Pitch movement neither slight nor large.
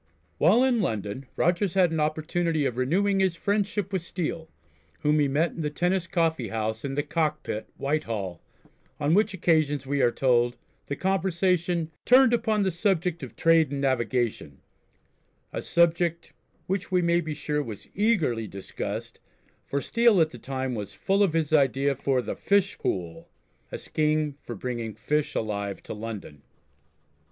No: wide, 5.7 semitones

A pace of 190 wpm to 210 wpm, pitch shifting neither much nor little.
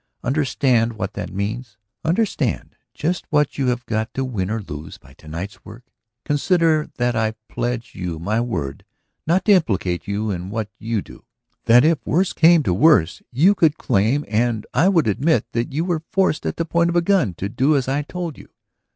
No: average, 195 wpm; wide, 7.0 semitones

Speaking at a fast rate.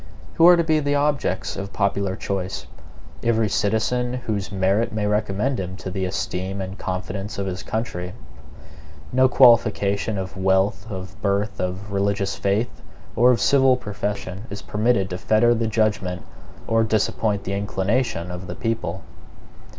No: average, 150 wpm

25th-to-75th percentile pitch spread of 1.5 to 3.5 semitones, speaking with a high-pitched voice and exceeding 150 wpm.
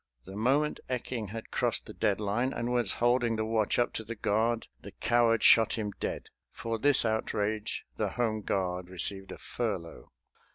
No: narrow, 2.6 semitones; low, 110 Hz; average, 175 wpm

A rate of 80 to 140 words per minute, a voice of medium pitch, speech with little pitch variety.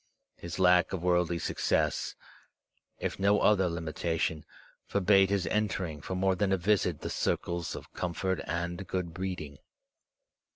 No: slow, 135 wpm; very low, 90 Hz; narrow, 2.0 semitones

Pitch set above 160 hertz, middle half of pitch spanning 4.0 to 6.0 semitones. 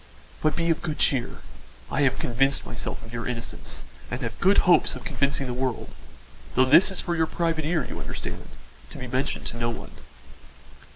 No: medium, 140 Hz; average, 4.8 semitones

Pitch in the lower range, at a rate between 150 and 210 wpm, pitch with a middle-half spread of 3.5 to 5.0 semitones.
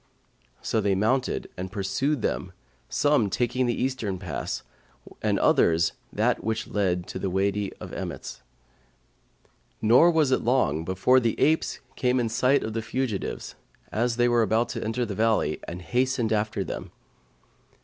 Yes: low, 110 Hz; average, 155 wpm; average, 4.3 semitones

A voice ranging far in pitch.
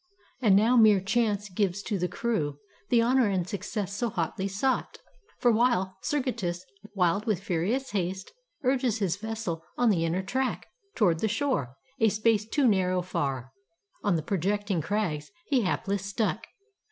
No: average, 4.0 semitones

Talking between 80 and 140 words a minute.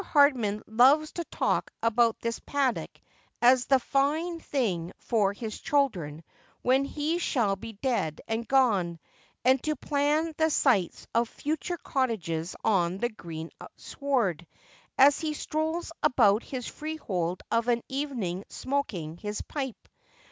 Yes: slow, 135 wpm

